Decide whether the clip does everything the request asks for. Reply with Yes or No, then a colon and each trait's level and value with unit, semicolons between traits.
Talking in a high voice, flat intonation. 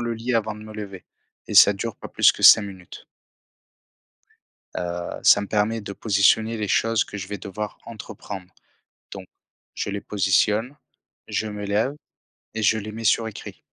No: low, 105 Hz; narrow, 1.9 semitones